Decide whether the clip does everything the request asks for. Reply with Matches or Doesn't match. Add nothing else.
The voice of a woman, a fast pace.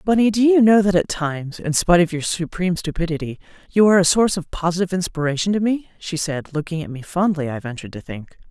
Matches